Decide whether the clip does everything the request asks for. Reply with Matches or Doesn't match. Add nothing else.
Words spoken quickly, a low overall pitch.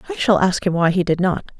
Doesn't match